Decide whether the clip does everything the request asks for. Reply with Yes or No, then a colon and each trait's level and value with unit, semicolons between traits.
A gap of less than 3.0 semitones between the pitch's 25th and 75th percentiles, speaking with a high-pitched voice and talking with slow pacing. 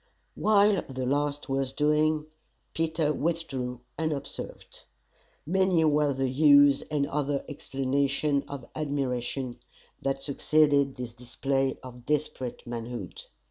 No: narrow, 2.5 semitones; medium, 140 Hz; slow, 105 wpm